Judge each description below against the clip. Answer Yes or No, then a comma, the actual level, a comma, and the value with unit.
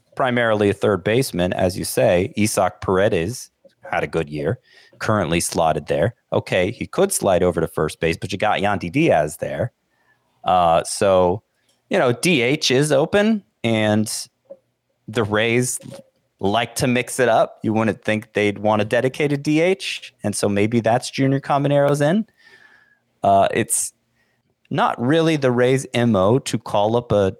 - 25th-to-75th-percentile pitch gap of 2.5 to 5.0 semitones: No, wide, 5.4 semitones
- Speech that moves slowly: No, average, 155 wpm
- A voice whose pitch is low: Yes, low, 120 Hz